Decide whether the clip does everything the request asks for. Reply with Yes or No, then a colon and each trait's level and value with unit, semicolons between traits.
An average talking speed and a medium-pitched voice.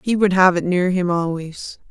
No: fast, 220 wpm; medium, 180 Hz